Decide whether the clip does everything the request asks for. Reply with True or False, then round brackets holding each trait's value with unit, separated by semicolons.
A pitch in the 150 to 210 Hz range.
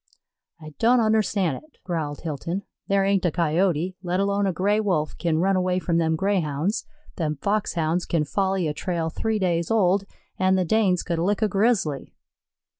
True (185 Hz)